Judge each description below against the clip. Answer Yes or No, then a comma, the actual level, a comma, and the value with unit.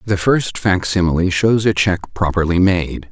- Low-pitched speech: Yes, very low, 95 Hz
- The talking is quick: No, average, 155 wpm